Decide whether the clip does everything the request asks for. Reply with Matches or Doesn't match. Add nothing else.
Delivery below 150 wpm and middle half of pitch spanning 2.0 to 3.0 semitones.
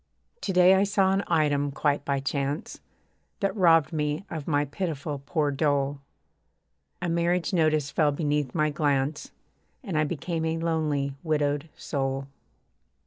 Matches